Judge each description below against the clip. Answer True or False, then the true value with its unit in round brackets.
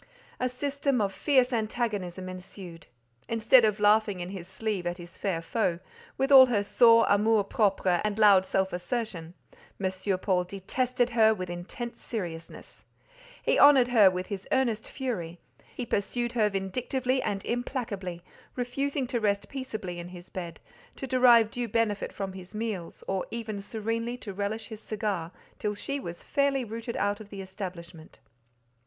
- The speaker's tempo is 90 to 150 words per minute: False (160 wpm)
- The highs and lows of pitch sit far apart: False (4.3 semitones)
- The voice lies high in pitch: True (210 Hz)